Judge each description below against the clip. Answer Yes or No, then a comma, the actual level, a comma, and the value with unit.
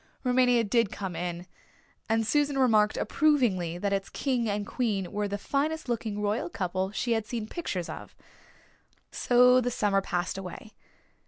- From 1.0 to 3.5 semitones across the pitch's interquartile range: No, average, 4.1 semitones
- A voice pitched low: No, high, 215 Hz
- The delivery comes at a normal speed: Yes, average, 155 wpm